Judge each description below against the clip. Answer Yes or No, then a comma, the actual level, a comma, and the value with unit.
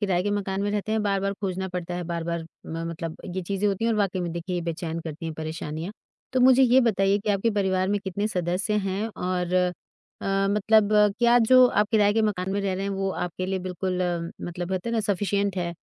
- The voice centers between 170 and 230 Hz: Yes, high, 190 Hz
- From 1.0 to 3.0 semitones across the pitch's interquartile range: Yes, narrow, 2.6 semitones